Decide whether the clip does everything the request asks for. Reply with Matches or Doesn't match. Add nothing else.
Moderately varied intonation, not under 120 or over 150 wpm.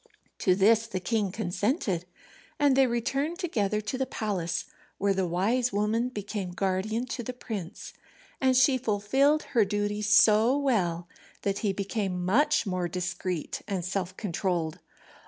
Matches